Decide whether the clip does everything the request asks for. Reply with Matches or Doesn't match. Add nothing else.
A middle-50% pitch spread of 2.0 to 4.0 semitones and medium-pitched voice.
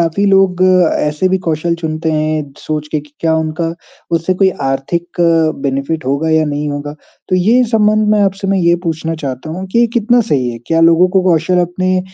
Matches